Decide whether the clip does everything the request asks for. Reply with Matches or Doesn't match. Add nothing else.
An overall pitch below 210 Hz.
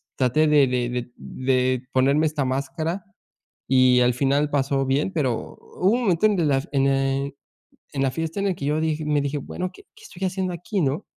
Matches